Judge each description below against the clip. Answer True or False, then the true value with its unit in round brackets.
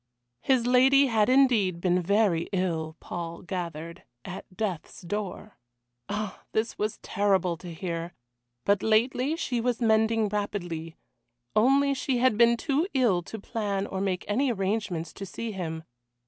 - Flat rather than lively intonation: False (4.6 semitones)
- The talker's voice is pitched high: True (205 Hz)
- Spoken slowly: False (145 wpm)